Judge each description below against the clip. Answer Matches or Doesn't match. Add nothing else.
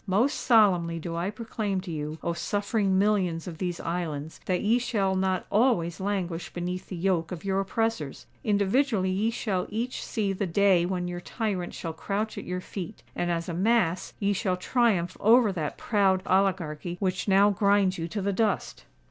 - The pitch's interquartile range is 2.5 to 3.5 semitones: Matches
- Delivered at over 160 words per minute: Matches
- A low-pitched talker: Doesn't match